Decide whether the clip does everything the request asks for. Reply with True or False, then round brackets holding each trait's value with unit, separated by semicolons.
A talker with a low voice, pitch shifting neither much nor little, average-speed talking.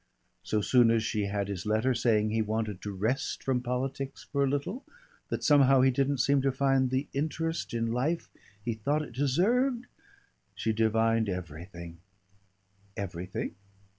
True (120 Hz; 4.7 semitones; 160 wpm)